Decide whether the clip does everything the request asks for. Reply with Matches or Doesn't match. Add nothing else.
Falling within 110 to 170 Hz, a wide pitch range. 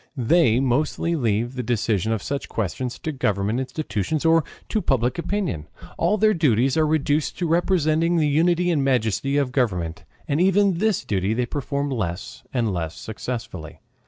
Matches